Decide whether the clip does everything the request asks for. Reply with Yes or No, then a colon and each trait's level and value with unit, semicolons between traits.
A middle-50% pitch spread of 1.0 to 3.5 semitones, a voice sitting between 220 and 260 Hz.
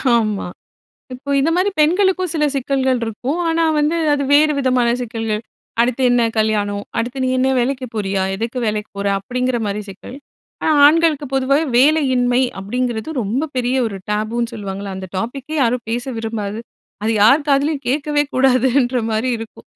No: average, 4.3 semitones; very high, 250 Hz